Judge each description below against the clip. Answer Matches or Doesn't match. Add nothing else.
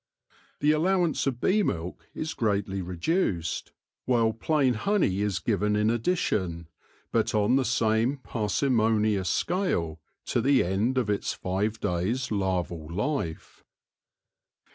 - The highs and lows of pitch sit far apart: Matches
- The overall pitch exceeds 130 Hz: Doesn't match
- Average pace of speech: Doesn't match